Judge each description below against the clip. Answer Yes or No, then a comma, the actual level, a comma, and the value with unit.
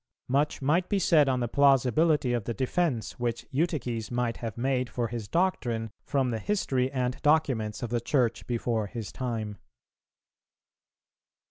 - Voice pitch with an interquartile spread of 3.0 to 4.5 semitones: Yes, average, 3.5 semitones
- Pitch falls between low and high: No, low, 125 Hz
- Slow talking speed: No, average, 150 wpm